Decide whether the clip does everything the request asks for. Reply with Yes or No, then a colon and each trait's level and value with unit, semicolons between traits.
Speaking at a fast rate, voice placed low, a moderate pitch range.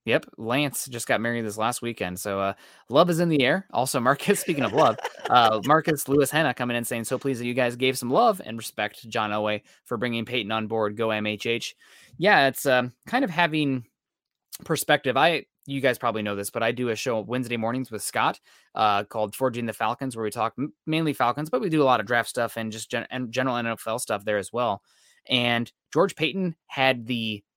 Yes: fast, 225 wpm; low, 120 Hz; average, 3.6 semitones